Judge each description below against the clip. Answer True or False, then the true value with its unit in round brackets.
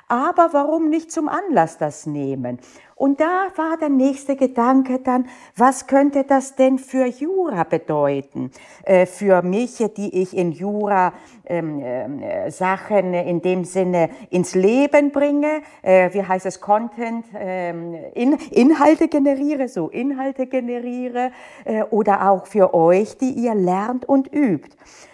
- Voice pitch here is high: True (245 Hz)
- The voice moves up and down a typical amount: False (7.3 semitones)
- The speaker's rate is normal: True (140 wpm)